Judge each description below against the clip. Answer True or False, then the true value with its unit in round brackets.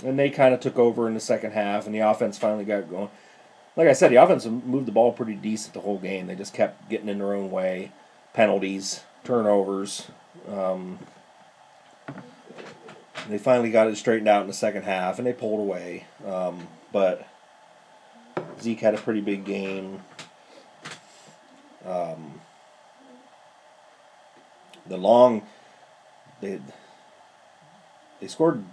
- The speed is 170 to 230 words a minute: False (140 wpm)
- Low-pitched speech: True (105 Hz)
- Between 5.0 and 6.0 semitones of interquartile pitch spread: False (2.8 semitones)